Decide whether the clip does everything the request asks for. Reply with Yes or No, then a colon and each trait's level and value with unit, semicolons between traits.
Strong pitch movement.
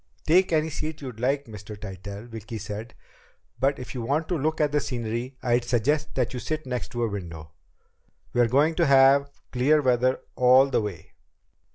No: average, 4.3 semitones